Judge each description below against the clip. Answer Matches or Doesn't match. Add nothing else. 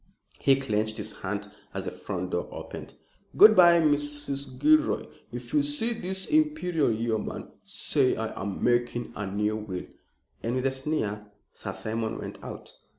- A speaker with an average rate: Matches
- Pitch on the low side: Matches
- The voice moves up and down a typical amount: Doesn't match